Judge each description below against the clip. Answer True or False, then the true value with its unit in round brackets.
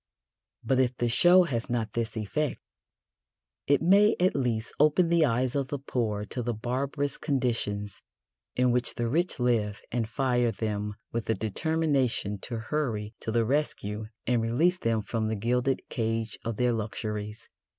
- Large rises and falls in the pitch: False (3.9 semitones)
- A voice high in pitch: False (120 Hz)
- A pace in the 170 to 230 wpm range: False (160 wpm)